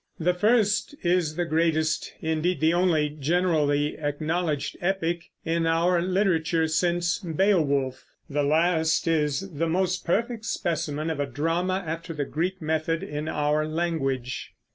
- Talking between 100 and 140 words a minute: Yes, slow, 135 wpm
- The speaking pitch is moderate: Yes, medium, 165 Hz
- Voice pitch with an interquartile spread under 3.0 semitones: Yes, narrow, 2.6 semitones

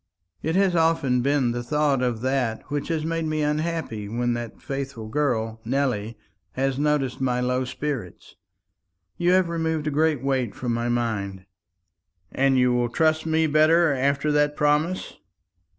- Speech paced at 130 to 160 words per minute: Yes, average, 155 wpm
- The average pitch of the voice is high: No, medium, 140 Hz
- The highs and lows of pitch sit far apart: No, average, 4.2 semitones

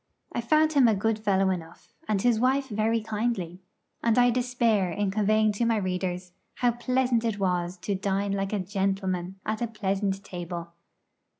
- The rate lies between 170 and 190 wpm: Yes, average, 175 wpm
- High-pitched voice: Yes, high, 205 Hz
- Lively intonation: No, average, 3.4 semitones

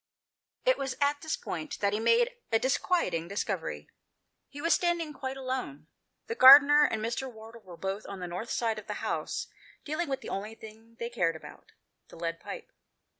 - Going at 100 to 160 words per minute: No, average, 195 wpm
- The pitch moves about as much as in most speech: No, wide, 6.2 semitones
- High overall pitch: Yes, high, 235 Hz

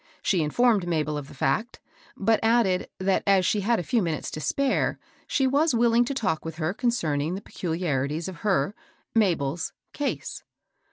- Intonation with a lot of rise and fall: Yes, wide, 6.6 semitones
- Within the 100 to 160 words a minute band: No, average, 180 wpm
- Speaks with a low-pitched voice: No, high, 190 Hz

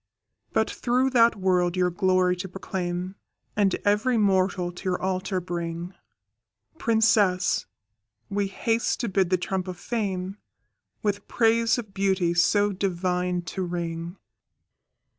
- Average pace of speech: No, slow, 125 wpm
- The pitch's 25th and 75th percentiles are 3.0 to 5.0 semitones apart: No, narrow, 2.4 semitones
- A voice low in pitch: No, high, 190 Hz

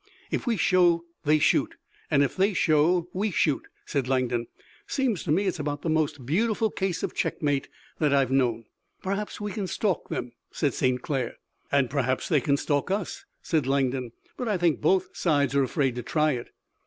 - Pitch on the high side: No, medium, 150 Hz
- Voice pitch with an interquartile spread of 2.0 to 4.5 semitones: No, average, 5.3 semitones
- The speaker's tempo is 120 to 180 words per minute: No, average, 190 wpm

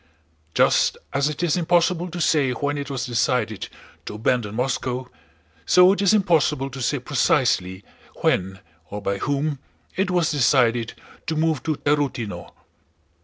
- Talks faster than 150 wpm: No, average, 145 wpm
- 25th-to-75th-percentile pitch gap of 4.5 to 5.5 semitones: Yes, average, 4.8 semitones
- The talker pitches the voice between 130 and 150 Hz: Yes, medium, 140 Hz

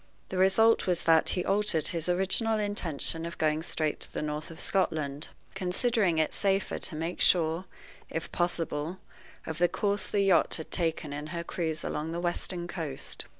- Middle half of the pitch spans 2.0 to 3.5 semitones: Yes, average, 3.1 semitones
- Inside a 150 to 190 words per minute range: Yes, average, 175 wpm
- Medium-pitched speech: Yes, medium, 170 Hz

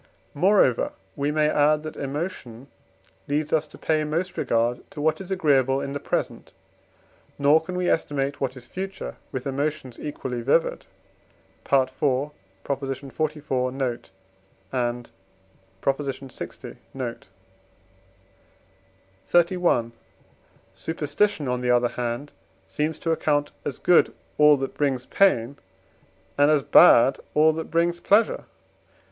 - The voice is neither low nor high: Yes, medium, 145 Hz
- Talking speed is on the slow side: Yes, slow, 120 wpm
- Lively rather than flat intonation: No, average, 3.3 semitones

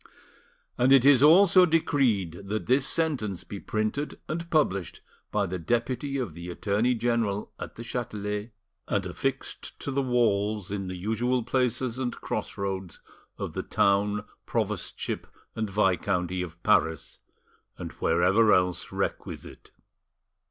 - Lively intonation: No, average, 4.8 semitones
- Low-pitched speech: Yes, low, 110 Hz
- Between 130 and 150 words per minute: Yes, slow, 135 wpm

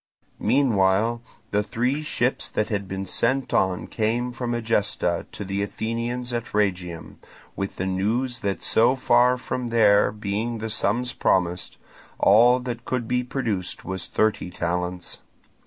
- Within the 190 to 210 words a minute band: No, average, 140 wpm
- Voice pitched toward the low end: Yes, low, 110 Hz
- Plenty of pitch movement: No, average, 3.9 semitones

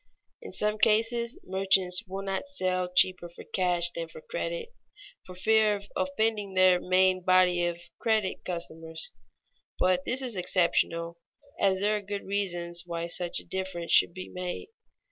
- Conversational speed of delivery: Yes, average, 160 wpm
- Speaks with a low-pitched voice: No, medium, 185 Hz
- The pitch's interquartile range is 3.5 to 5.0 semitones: No, average, 2.7 semitones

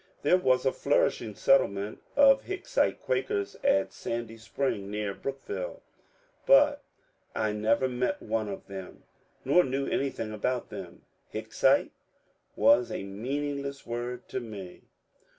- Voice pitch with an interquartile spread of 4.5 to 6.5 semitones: Yes, average, 5.2 semitones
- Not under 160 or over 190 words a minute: No, slow, 135 wpm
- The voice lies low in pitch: Yes, low, 125 Hz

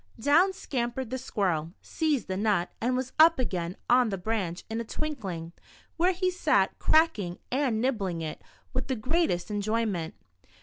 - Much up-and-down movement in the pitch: Yes, wide, 6.6 semitones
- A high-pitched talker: Yes, high, 230 Hz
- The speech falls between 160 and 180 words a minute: Yes, average, 165 wpm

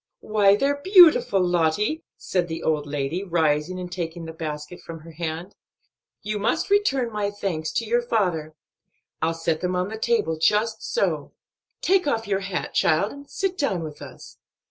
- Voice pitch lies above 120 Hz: Yes, medium, 185 Hz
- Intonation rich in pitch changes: Yes, wide, 5.7 semitones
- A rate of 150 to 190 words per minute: Yes, average, 175 wpm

